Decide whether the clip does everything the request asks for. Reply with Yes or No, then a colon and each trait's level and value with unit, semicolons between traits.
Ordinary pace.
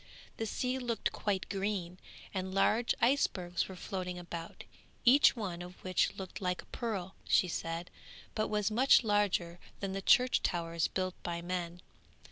Yes: average, 155 wpm